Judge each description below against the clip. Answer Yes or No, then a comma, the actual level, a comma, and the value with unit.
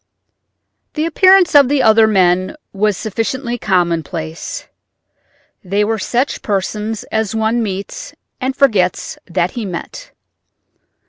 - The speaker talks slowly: Yes, slow, 115 wpm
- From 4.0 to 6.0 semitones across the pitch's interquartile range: Yes, average, 4.5 semitones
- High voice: Yes, high, 215 Hz